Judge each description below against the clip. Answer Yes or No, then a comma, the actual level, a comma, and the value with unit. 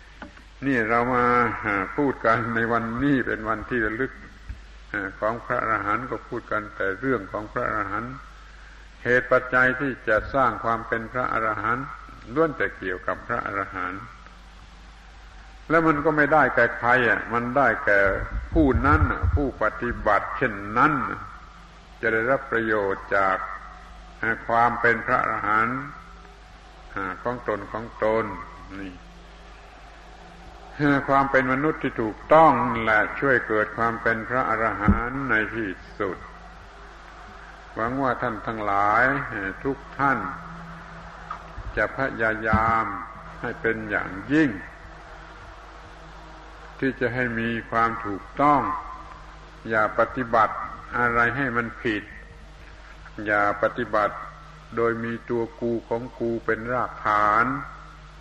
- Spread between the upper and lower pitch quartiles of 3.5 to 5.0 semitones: No, average, 2.7 semitones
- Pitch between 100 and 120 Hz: Yes, low, 115 Hz